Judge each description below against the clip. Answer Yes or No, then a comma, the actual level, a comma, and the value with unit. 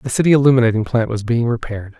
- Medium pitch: No, low, 120 Hz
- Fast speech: Yes, fast, 210 wpm